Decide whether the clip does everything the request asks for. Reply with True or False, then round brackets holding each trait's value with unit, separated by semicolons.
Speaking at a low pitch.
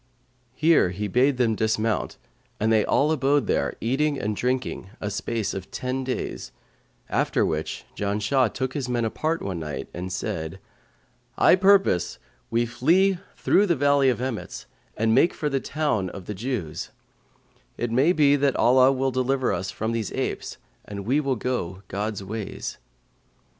True (120 Hz)